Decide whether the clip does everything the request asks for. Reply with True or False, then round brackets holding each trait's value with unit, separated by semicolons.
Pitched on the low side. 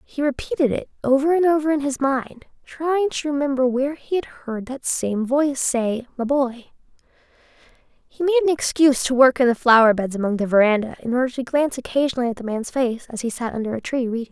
False (260 Hz)